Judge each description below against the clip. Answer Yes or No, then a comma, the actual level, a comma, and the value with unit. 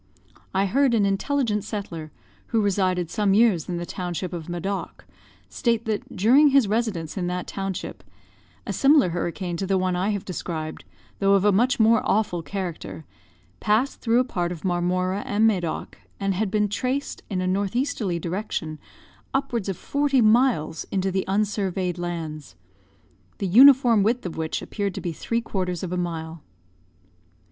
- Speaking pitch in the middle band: No, high, 195 Hz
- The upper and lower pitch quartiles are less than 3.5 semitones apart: No, average, 3.9 semitones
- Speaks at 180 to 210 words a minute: No, average, 165 wpm